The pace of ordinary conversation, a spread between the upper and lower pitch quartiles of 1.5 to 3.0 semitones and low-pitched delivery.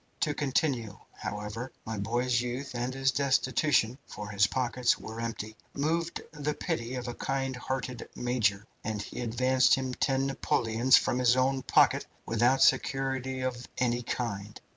Yes: average, 150 wpm; narrow, 2.5 semitones; low, 125 Hz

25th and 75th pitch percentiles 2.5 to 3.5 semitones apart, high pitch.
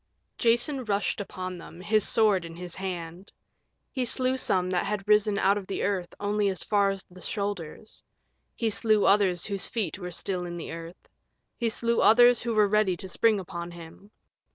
Yes: average, 3.1 semitones; high, 200 Hz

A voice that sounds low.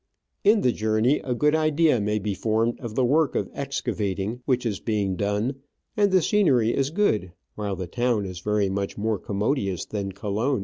Yes: low, 110 Hz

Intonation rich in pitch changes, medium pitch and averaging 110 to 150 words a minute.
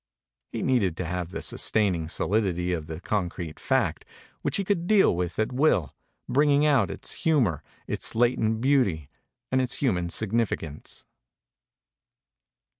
No: wide, 7.1 semitones; low, 110 Hz; slow, 135 wpm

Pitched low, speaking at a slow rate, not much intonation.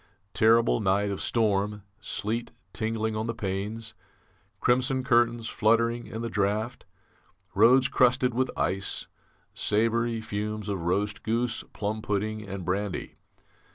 Yes: low, 110 Hz; slow, 120 wpm; narrow, 2.2 semitones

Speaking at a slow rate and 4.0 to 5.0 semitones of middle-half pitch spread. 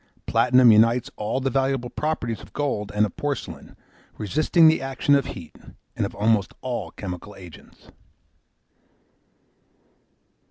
Yes: slow, 125 wpm; average, 4.4 semitones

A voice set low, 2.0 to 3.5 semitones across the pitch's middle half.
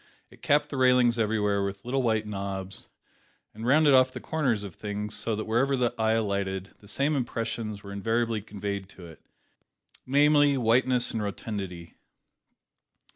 No: low, 110 Hz; average, 4.1 semitones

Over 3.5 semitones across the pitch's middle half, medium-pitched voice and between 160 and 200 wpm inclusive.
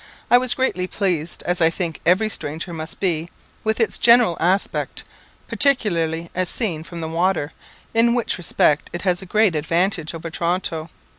Yes: average, 3.9 semitones; medium, 175 Hz; average, 165 wpm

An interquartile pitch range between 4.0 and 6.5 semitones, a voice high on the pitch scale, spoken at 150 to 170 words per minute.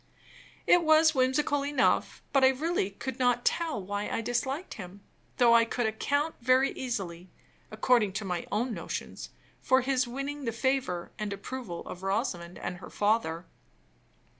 Yes: average, 5.0 semitones; high, 240 Hz; average, 155 wpm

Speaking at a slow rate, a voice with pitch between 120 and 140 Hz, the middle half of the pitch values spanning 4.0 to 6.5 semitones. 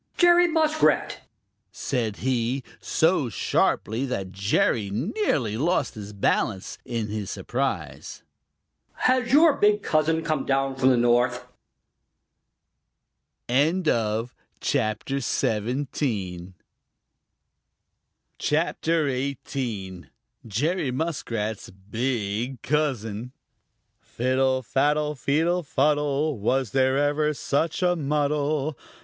Yes: slow, 85 wpm; low, 135 Hz; average, 5.1 semitones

